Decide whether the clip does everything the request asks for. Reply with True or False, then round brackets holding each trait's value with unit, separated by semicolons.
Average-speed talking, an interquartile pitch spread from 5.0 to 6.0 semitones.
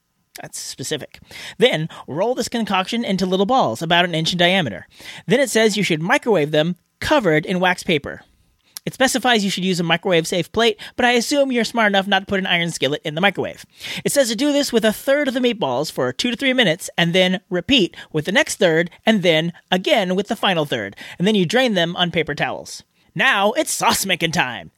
False (225 wpm; 5.5 semitones)